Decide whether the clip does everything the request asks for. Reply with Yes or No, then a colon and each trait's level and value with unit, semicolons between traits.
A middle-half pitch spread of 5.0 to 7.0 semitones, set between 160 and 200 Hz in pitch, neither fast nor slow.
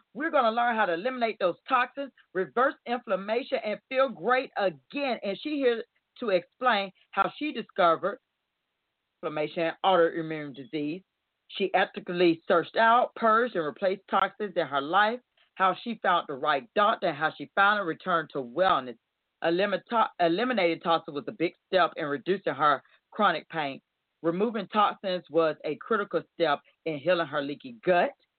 Yes: average, 5.3 semitones; high, 190 Hz; average, 155 wpm